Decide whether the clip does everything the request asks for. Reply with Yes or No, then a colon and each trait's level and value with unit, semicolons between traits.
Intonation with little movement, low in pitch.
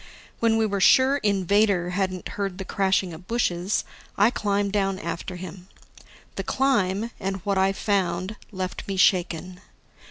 No: narrow, 2.0 semitones; high, 195 Hz